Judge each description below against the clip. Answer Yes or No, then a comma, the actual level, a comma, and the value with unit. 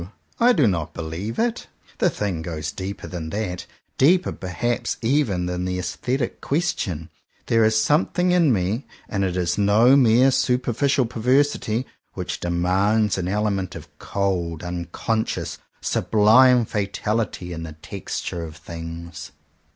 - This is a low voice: Yes, low, 100 Hz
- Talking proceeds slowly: No, average, 145 wpm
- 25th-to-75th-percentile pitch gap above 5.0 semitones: Yes, wide, 5.6 semitones